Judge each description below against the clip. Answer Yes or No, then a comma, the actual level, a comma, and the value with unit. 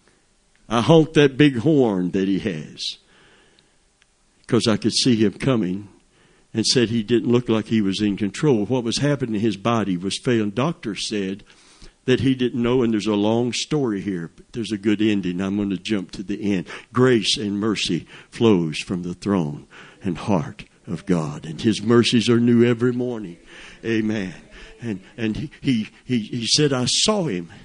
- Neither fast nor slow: Yes, average, 180 wpm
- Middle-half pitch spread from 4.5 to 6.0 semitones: No, average, 3.4 semitones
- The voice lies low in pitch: Yes, low, 110 Hz